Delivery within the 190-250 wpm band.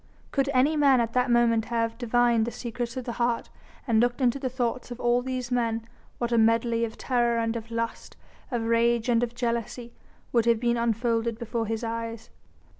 Yes: average, 195 wpm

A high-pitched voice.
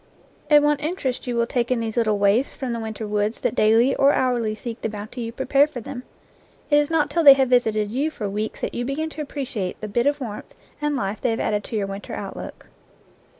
Yes: high, 240 Hz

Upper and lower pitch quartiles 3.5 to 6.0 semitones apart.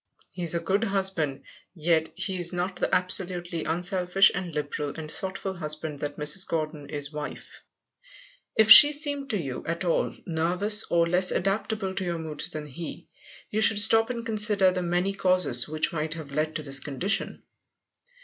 Yes: average, 3.9 semitones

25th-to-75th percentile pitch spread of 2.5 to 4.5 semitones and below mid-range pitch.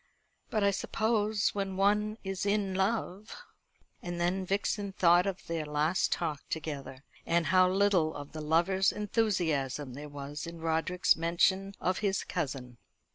No: average, 4.0 semitones; medium, 180 Hz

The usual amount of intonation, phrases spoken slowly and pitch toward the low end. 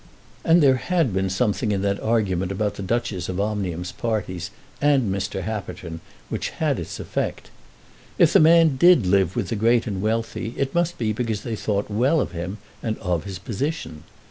No: average, 4.4 semitones; average, 185 wpm; low, 105 Hz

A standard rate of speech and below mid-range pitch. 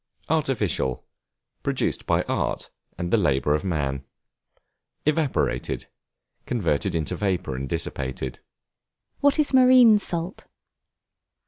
No: slow, 100 wpm; very low, 95 Hz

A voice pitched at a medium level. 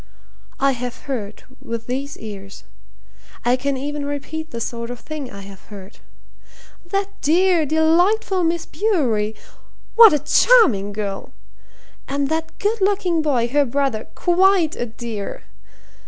No: very high, 280 Hz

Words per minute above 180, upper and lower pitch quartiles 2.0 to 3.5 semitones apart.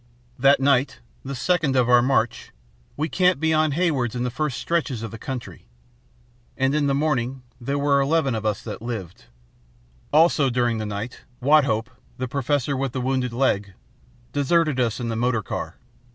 No: average, 165 wpm; average, 3.2 semitones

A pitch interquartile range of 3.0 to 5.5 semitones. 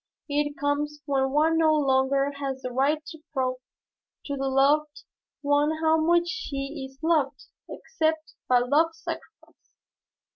No: narrow, 2.5 semitones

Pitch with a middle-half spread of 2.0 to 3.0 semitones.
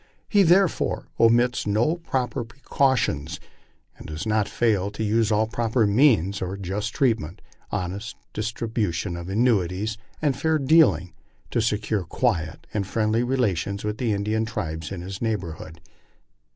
No: average, 3.8 semitones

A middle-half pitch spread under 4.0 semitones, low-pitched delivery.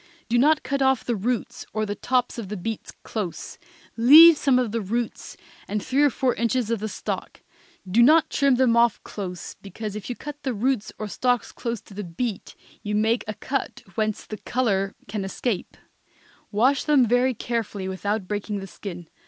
No: average, 3.6 semitones; high, 230 Hz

